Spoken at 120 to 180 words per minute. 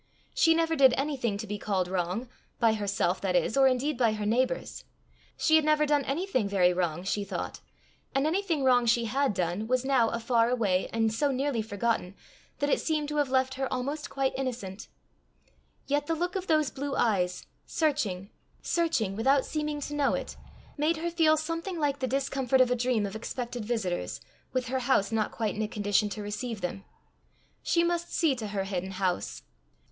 No: average, 190 wpm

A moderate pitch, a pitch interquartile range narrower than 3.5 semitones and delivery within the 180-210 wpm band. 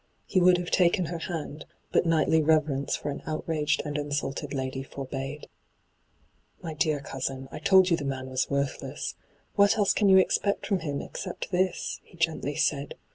No: medium, 155 Hz; average, 4.1 semitones; average, 185 wpm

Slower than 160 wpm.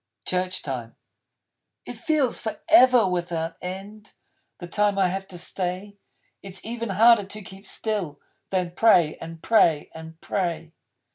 Yes: slow, 135 wpm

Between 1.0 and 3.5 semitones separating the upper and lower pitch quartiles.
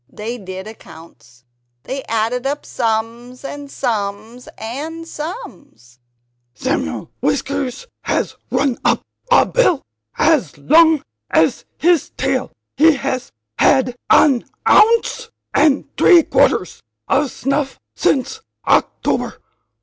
No: average, 5.1 semitones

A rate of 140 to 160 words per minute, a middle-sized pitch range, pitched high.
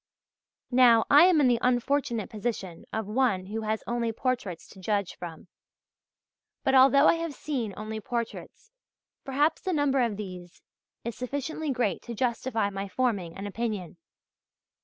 Yes: average, 150 wpm; average, 4.6 semitones; high, 235 Hz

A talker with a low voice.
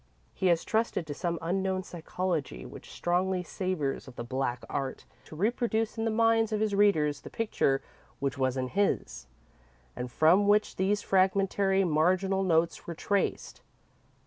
No: medium, 185 Hz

